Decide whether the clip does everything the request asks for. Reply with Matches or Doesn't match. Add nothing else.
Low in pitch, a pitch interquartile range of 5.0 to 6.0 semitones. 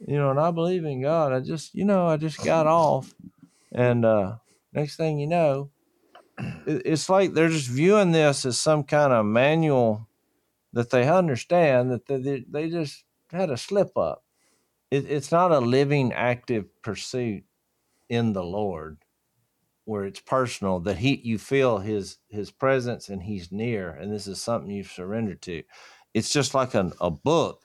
Matches